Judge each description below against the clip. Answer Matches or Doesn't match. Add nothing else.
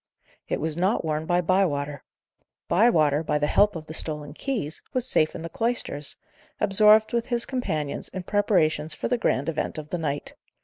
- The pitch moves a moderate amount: Doesn't match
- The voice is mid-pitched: Matches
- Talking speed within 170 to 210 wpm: Matches